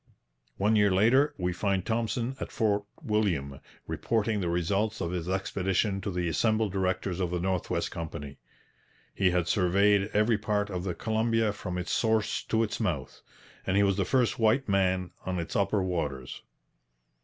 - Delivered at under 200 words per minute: Yes, average, 170 wpm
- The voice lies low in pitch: Yes, low, 100 Hz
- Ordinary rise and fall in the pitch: Yes, average, 3.3 semitones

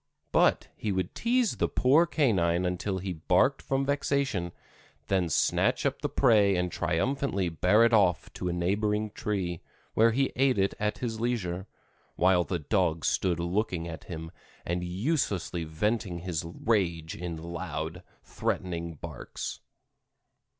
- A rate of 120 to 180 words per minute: Yes, average, 145 wpm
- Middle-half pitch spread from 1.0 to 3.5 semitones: No, average, 4.4 semitones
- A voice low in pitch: Yes, very low, 95 Hz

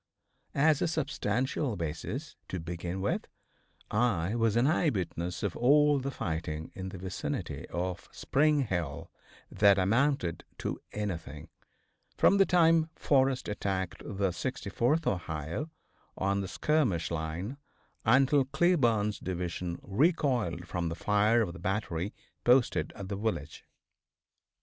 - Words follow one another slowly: Yes, slow, 125 wpm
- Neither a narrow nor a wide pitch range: No, wide, 7.3 semitones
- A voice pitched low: Yes, low, 100 Hz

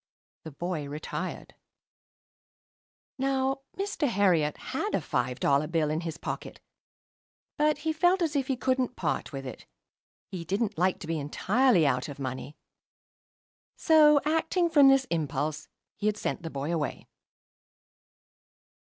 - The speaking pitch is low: No, medium, 185 Hz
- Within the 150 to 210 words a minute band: No, average, 140 wpm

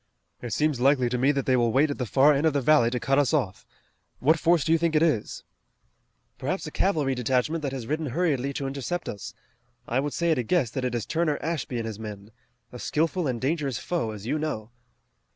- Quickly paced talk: Yes, fast, 235 wpm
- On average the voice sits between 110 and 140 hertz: Yes, low, 135 Hz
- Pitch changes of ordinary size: Yes, average, 4.3 semitones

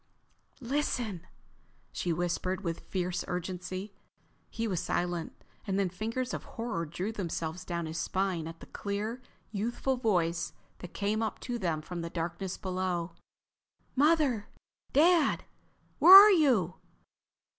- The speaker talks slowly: Yes, slow, 130 wpm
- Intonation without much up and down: No, average, 4.8 semitones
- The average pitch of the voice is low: No, high, 190 Hz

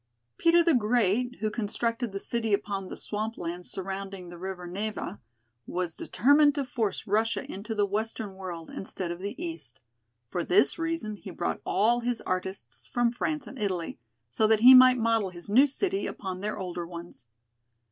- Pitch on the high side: Yes, high, 205 Hz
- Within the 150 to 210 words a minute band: Yes, average, 175 wpm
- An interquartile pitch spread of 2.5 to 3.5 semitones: No, average, 4.4 semitones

